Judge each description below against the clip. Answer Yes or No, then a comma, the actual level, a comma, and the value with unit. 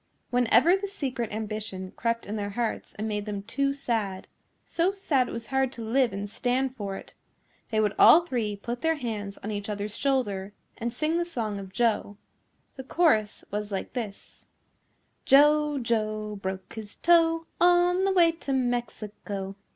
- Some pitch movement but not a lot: Yes, average, 5.0 semitones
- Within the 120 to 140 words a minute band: No, average, 170 wpm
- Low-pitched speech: No, high, 230 Hz